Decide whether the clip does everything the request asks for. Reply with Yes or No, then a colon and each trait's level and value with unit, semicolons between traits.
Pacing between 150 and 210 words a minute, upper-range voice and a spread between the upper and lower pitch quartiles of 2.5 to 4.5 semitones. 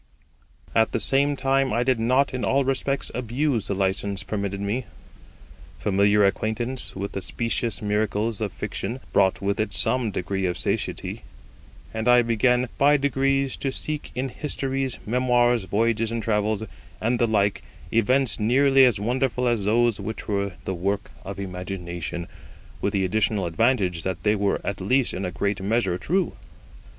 No: average, 160 wpm; low, 110 Hz; average, 4.2 semitones